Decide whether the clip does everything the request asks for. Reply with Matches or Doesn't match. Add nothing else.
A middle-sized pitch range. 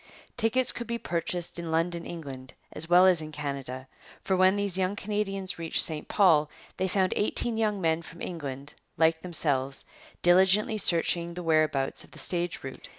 Matches